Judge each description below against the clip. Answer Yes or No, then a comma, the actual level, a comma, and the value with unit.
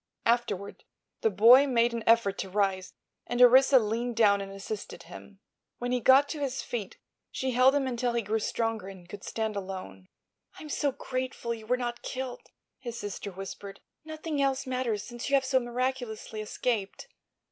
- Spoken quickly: No, average, 175 wpm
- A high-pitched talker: Yes, high, 235 Hz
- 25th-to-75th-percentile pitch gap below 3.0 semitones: No, average, 3.9 semitones